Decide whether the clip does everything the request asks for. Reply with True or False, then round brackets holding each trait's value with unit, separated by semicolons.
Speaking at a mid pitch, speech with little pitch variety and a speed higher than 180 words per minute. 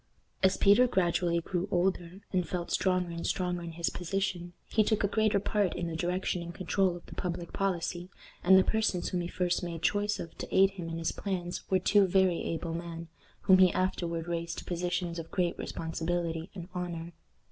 True (175 Hz; 1.9 semitones; 200 wpm)